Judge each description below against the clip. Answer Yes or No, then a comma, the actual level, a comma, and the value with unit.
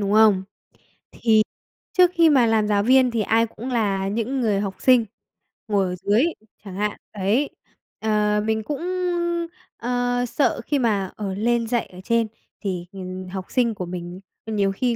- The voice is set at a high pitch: Yes, high, 215 Hz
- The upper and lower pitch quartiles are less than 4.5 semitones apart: Yes, average, 3.4 semitones